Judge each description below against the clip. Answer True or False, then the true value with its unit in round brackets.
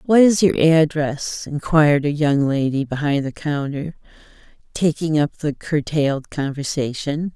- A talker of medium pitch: True (150 Hz)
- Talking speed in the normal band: False (130 wpm)